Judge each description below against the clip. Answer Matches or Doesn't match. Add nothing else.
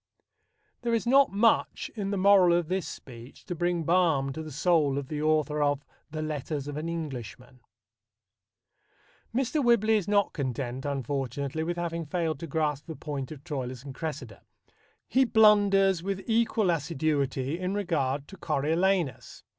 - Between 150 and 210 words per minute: Matches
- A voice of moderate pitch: Matches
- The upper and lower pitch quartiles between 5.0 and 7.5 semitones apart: Matches